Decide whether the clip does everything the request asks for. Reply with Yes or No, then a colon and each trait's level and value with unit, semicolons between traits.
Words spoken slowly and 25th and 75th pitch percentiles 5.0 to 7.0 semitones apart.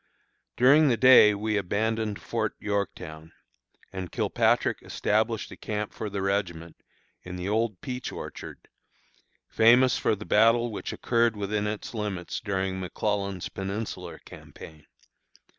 No: slow, 125 wpm; average, 2.7 semitones